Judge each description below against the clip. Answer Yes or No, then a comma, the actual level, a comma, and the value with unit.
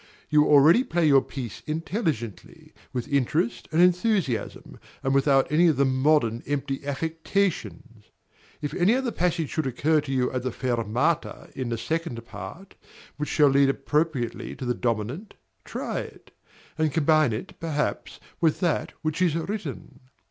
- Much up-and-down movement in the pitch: No, average, 4.2 semitones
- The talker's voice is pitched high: No, medium, 145 Hz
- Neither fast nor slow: Yes, average, 150 wpm